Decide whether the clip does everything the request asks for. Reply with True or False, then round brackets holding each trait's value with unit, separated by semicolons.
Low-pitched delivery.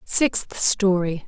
False (190 Hz)